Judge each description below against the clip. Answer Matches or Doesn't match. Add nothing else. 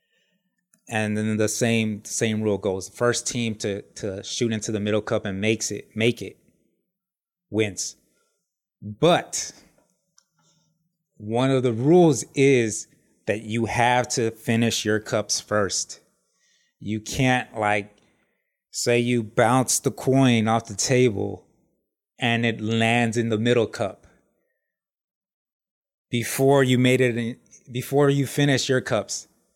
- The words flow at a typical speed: Doesn't match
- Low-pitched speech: Matches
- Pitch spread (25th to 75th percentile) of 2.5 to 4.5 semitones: Matches